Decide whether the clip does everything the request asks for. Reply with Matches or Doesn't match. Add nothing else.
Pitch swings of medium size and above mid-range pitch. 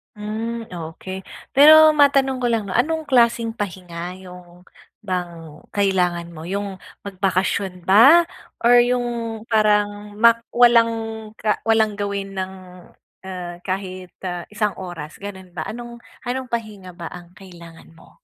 Matches